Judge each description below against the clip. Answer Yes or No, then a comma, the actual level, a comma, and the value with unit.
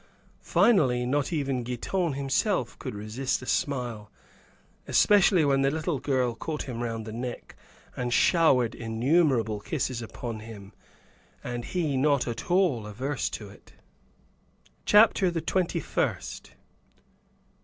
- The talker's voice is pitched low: Yes, low, 130 Hz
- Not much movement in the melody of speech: No, average, 5.0 semitones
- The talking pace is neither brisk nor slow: No, slow, 125 wpm